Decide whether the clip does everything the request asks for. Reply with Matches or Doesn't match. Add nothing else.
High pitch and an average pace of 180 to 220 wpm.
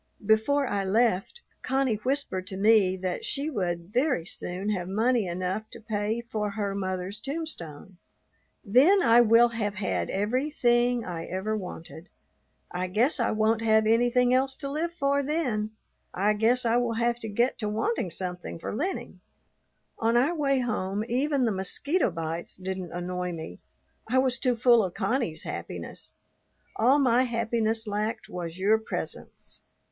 Doesn't match